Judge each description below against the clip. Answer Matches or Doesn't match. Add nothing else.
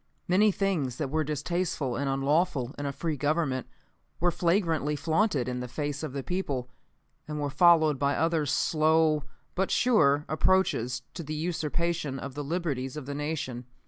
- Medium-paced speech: Matches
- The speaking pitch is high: Doesn't match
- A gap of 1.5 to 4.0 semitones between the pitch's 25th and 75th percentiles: Matches